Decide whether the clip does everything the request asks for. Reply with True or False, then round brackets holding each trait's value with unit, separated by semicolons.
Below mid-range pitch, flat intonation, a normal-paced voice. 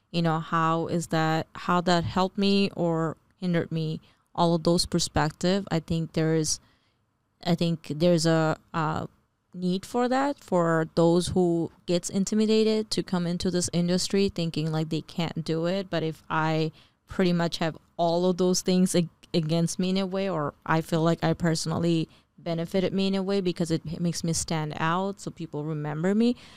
False (170 Hz; 2.2 semitones; 180 wpm)